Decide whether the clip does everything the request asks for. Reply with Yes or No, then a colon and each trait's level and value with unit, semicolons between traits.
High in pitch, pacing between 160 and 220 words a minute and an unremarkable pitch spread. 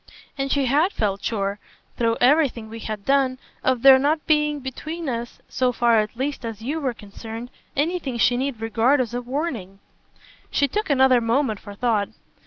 Yes: very high, 250 Hz; average, 180 wpm; average, 3.8 semitones